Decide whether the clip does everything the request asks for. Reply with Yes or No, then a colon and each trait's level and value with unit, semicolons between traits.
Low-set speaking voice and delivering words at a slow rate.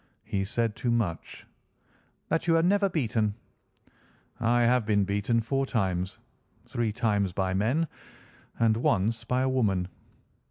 Yes: low, 115 Hz; slow, 130 wpm